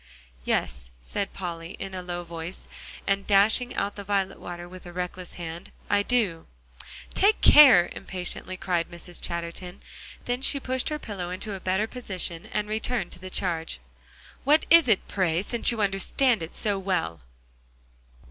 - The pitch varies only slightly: No, average, 3.5 semitones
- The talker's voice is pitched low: No, high, 190 Hz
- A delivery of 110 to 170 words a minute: Yes, average, 160 wpm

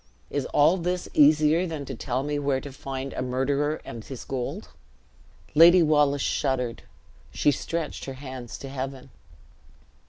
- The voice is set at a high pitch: No, medium, 140 Hz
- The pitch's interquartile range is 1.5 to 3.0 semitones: Yes, narrow, 2.4 semitones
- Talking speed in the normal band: Yes, average, 150 wpm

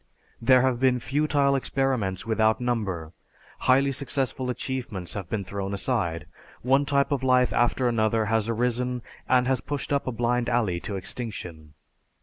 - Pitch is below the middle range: Yes, low, 120 Hz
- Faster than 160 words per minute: No, average, 150 wpm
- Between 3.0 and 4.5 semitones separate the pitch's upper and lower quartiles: Yes, average, 3.6 semitones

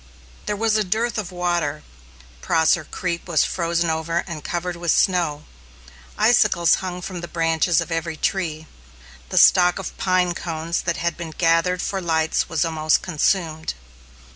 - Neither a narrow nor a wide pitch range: No, narrow, 2.0 semitones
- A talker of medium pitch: Yes, medium, 170 Hz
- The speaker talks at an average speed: Yes, average, 155 wpm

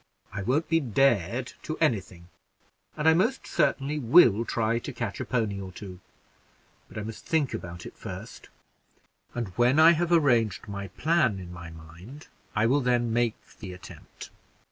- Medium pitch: No, low, 115 Hz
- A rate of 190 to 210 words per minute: No, average, 170 wpm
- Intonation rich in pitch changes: Yes, wide, 6.7 semitones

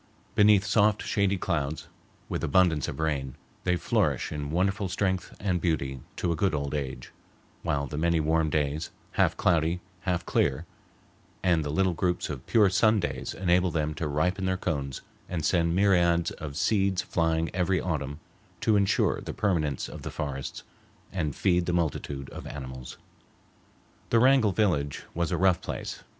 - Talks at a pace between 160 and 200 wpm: Yes, average, 165 wpm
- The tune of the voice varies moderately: Yes, average, 4.0 semitones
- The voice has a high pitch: No, very low, 85 Hz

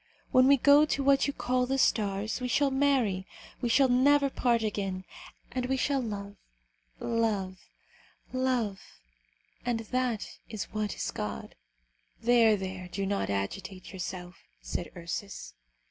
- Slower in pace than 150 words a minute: Yes, average, 140 wpm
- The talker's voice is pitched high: Yes, high, 225 Hz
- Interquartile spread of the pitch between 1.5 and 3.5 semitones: No, average, 4.8 semitones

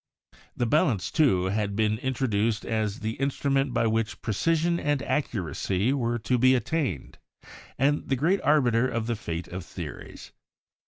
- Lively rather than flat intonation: No, average, 4.5 semitones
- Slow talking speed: No, average, 160 wpm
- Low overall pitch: Yes, low, 115 Hz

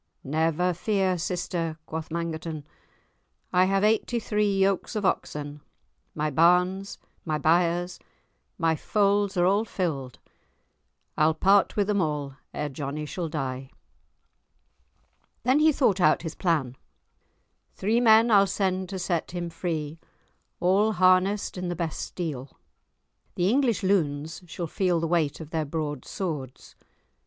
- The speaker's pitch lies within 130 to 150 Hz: No, medium, 175 Hz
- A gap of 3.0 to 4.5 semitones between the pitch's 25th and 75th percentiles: Yes, average, 3.9 semitones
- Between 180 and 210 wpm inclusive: No, slow, 135 wpm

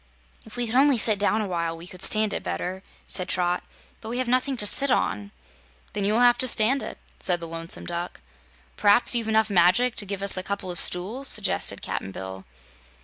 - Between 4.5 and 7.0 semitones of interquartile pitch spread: Yes, average, 5.1 semitones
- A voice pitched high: Yes, high, 205 Hz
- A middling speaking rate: No, fast, 215 wpm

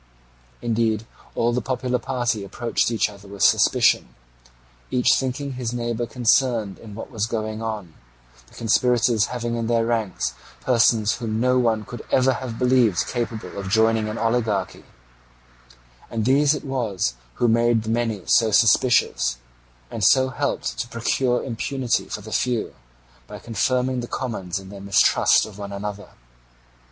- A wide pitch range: No, narrow, 2.5 semitones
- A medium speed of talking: Yes, average, 150 wpm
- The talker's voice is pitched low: Yes, low, 115 Hz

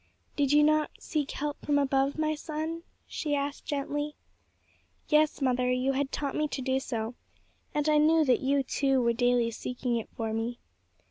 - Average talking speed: Yes, average, 180 wpm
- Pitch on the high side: Yes, very high, 280 Hz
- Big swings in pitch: No, average, 3.0 semitones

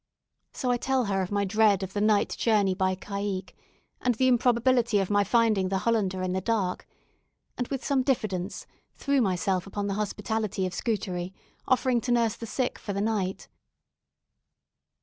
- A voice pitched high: Yes, high, 205 Hz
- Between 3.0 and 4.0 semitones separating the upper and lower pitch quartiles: Yes, average, 3.7 semitones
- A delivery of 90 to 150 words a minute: No, average, 170 wpm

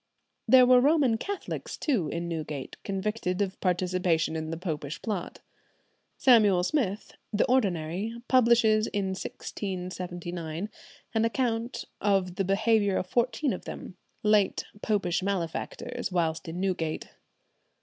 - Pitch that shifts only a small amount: No, average, 4.4 semitones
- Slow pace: Yes, slow, 120 wpm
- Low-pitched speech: No, high, 195 Hz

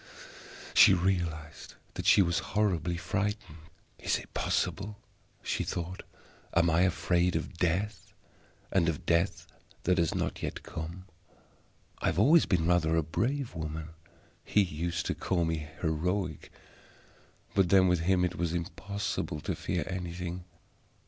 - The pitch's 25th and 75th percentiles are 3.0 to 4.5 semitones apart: No, narrow, 2.5 semitones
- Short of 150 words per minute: Yes, average, 140 wpm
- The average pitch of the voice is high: No, very low, 90 Hz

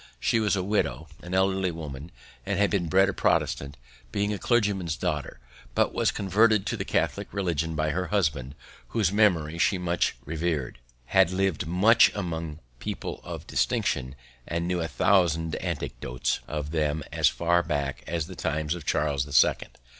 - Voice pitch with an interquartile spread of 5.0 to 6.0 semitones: No, average, 4.2 semitones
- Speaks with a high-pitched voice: No, very low, 85 Hz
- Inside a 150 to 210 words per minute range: Yes, average, 165 wpm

